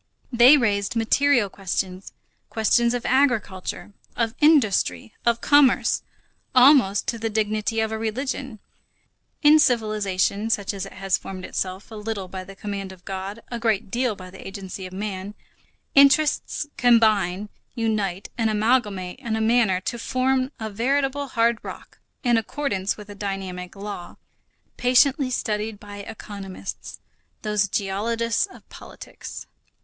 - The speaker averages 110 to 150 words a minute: Yes, average, 140 wpm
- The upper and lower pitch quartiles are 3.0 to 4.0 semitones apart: Yes, average, 3.6 semitones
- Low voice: No, high, 215 Hz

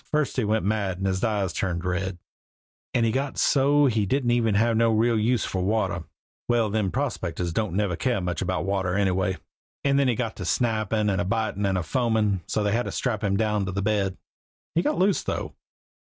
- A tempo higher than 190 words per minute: Yes, fast, 205 wpm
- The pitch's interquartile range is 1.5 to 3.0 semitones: No, average, 3.6 semitones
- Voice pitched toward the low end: Yes, low, 105 Hz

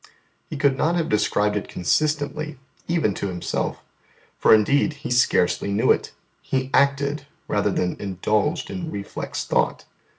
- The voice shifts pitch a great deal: Yes, wide, 6.8 semitones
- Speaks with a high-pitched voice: No, medium, 140 Hz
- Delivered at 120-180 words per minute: Yes, average, 140 wpm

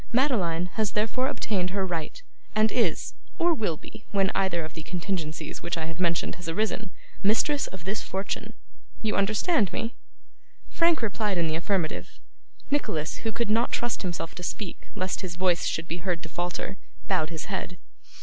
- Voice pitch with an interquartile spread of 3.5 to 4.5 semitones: Yes, average, 4.2 semitones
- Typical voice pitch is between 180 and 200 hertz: Yes, high, 190 Hz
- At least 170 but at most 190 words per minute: Yes, average, 175 wpm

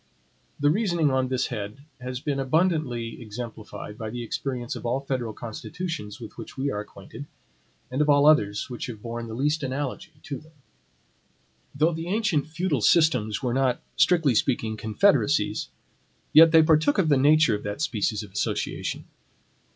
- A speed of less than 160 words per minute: No, average, 165 wpm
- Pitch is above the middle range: No, low, 130 Hz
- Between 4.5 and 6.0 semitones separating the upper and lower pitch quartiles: Yes, average, 5.2 semitones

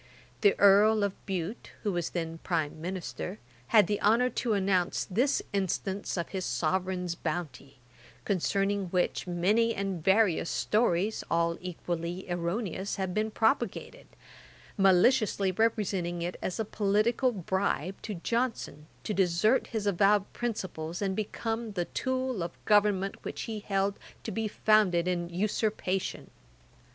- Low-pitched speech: No, high, 195 Hz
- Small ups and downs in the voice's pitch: No, average, 3.4 semitones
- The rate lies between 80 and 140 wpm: Yes, slow, 135 wpm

